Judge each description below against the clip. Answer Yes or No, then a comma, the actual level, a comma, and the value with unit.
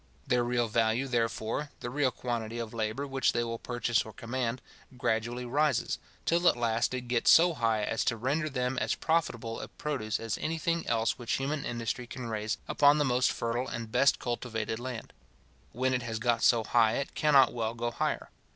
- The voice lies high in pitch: No, low, 120 Hz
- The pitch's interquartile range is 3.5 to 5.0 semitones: No, narrow, 2.6 semitones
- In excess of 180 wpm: Yes, average, 195 wpm